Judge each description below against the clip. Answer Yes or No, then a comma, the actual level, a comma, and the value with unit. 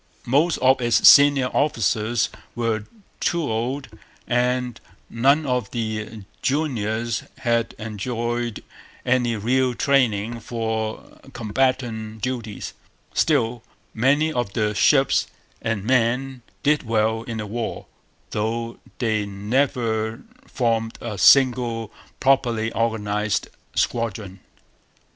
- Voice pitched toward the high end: No, low, 115 Hz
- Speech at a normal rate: No, slow, 100 wpm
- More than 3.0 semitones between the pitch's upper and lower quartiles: No, narrow, 2.6 semitones